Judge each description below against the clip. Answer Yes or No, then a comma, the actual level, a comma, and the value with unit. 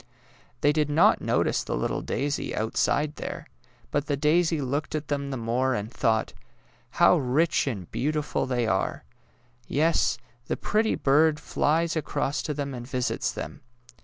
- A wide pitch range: No, average, 3.2 semitones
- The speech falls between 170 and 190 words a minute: No, average, 160 wpm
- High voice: No, medium, 145 Hz